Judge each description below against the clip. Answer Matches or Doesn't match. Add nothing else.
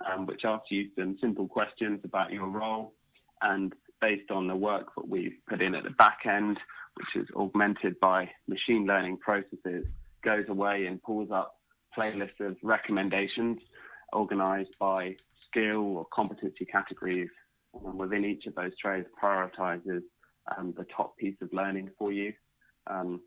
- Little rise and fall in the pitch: Matches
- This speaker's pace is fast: Doesn't match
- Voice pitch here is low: Matches